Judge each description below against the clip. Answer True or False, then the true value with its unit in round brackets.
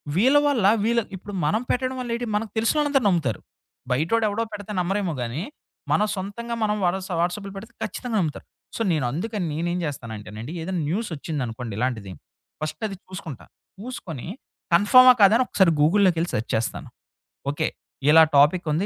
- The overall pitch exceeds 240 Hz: False (185 Hz)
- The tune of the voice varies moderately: False (6.4 semitones)